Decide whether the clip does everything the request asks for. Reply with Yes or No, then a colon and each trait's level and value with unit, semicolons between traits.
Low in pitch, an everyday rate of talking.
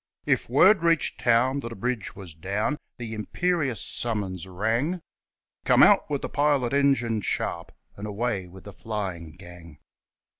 Yes: low, 115 Hz; average, 150 wpm